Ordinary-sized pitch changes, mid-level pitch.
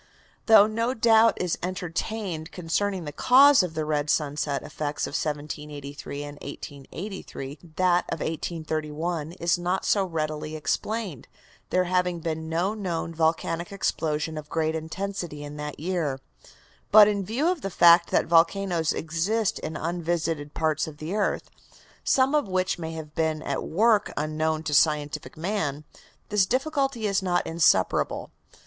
Yes: average, 4.1 semitones; medium, 165 Hz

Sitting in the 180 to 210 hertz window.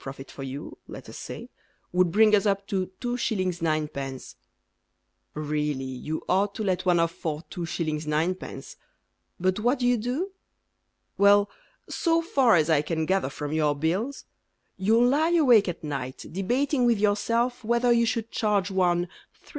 Yes: high, 190 Hz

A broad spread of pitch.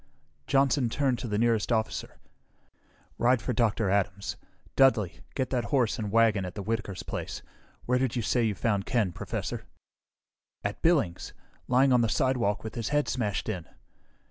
No: average, 3.5 semitones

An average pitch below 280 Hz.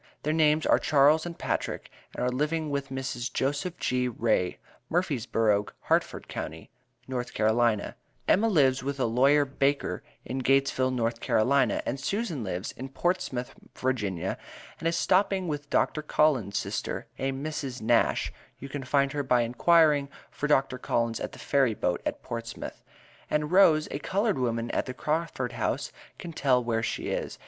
Yes: low, 135 Hz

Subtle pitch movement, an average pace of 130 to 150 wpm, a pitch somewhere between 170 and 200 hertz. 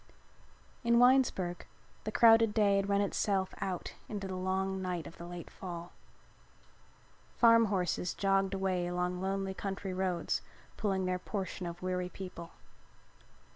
Yes: narrow, 1.8 semitones; slow, 135 wpm; high, 190 Hz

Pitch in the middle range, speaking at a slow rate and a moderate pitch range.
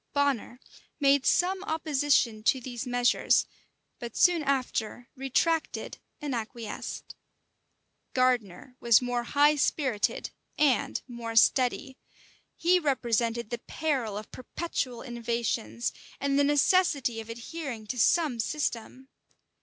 No: very high, 255 Hz; slow, 110 wpm; average, 3.6 semitones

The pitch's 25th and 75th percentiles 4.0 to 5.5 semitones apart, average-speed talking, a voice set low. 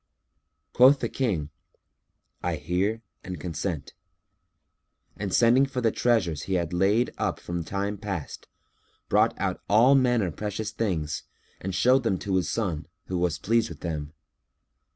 Yes: average, 4.9 semitones; average, 145 wpm; low, 100 Hz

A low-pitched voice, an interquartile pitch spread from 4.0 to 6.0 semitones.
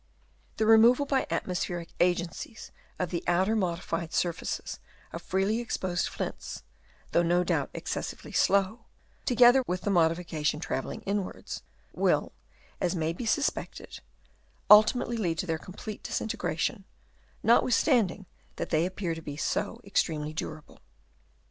No: medium, 185 Hz; average, 4.6 semitones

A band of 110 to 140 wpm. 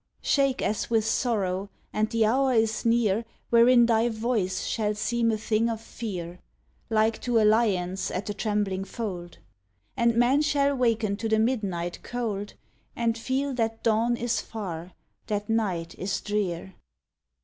No: average, 150 wpm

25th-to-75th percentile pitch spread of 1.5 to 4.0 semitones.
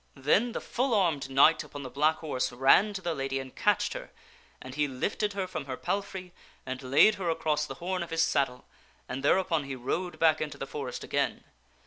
No: average, 5.3 semitones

